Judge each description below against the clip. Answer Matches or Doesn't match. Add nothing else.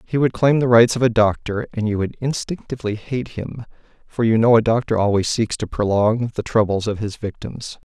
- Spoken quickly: Matches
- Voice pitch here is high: Doesn't match